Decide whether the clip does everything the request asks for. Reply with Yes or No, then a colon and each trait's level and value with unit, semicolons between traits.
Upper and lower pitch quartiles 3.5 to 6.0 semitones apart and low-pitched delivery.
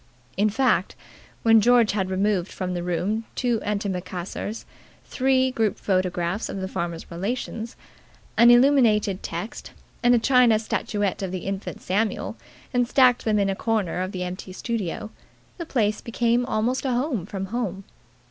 No: average, 4.2 semitones; high, 210 Hz